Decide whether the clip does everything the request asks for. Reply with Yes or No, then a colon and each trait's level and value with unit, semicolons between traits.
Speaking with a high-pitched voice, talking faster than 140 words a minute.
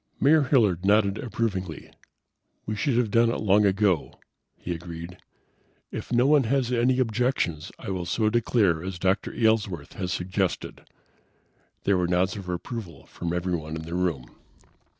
No: very low, 95 Hz; average, 150 wpm